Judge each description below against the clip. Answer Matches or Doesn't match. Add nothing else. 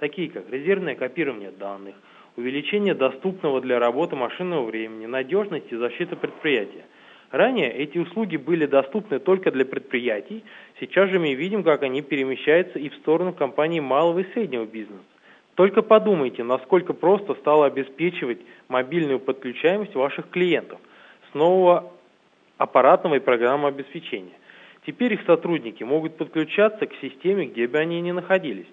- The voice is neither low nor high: Matches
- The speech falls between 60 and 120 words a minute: Doesn't match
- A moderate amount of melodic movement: Doesn't match